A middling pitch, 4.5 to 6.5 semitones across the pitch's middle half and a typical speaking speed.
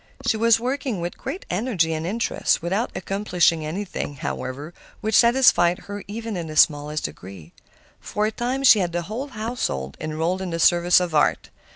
Yes: medium, 180 Hz; wide, 5.6 semitones; average, 175 wpm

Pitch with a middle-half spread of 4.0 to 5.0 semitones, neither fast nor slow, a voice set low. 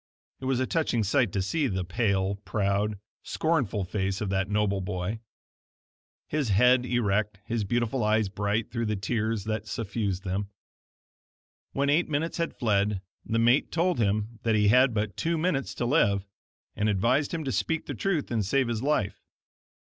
Yes: average, 4.5 semitones; average, 170 wpm; low, 110 Hz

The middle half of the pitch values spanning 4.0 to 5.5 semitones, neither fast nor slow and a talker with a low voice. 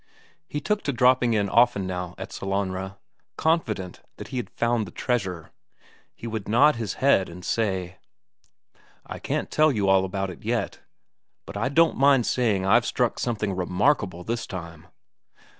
Yes: average, 4.8 semitones; average, 160 wpm; low, 105 Hz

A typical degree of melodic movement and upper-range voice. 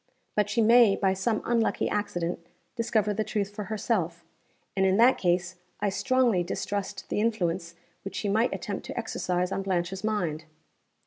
Yes: average, 3.1 semitones; high, 200 Hz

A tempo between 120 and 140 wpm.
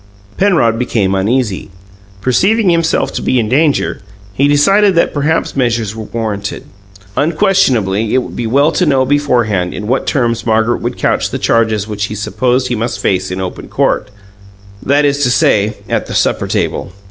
No: average, 170 wpm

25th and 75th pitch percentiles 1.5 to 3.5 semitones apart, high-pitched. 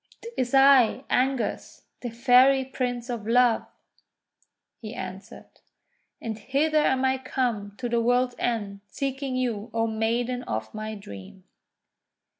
Yes: average, 2.9 semitones; high, 245 Hz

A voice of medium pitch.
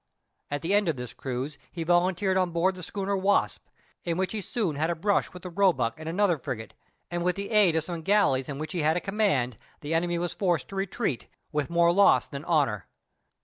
Yes: medium, 170 Hz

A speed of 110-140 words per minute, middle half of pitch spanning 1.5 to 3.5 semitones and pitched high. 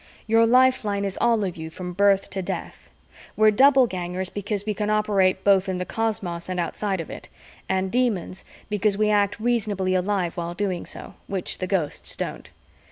No: average, 175 wpm; narrow, 2.5 semitones; high, 200 Hz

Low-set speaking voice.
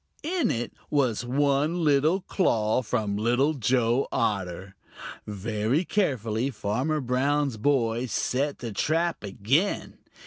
Yes: low, 125 Hz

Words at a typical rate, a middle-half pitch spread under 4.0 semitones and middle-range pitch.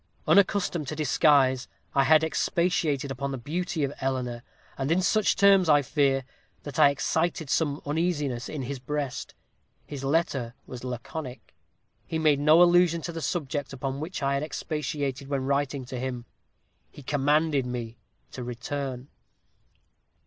Yes: average, 150 wpm; average, 3.2 semitones; medium, 145 Hz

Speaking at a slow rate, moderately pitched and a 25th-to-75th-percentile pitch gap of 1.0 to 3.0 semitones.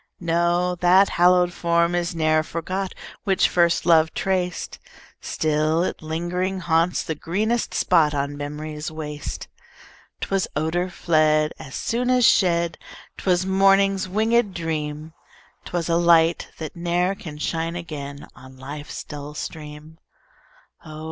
Yes: slow, 130 wpm; medium, 170 Hz; average, 2.7 semitones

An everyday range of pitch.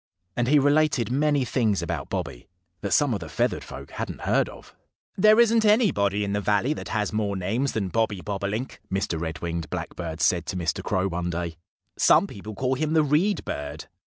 No: wide, 7.7 semitones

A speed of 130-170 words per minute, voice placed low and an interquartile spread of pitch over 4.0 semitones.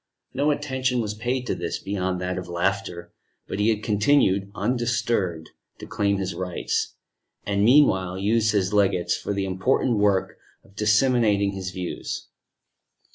No: average, 145 wpm; low, 100 Hz; average, 3.6 semitones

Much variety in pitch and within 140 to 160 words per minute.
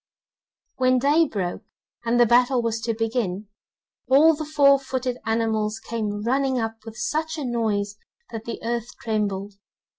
No: average, 3.2 semitones; average, 150 wpm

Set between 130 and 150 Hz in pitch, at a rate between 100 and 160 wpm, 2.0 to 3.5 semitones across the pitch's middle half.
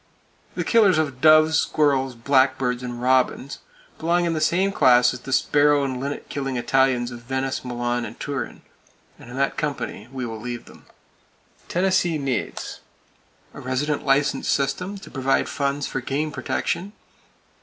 Yes: low, 135 Hz; average, 155 wpm; average, 3.2 semitones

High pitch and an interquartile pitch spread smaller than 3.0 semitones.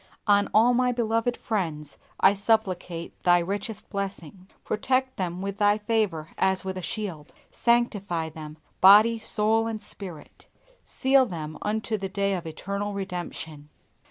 No: high, 200 Hz; average, 3.9 semitones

